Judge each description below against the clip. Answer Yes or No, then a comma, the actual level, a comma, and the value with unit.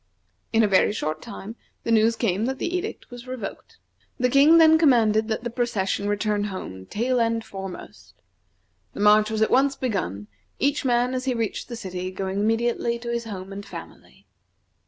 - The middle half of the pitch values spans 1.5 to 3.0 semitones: No, average, 3.4 semitones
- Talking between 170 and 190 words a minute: Yes, average, 180 wpm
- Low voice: No, high, 225 Hz